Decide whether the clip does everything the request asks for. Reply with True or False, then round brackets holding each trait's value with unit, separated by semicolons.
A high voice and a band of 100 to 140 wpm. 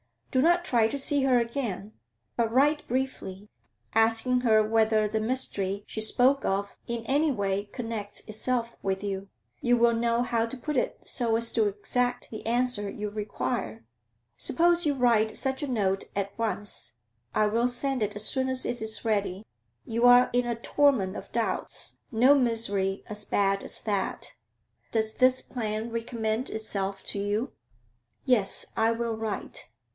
False (225 Hz; 165 wpm)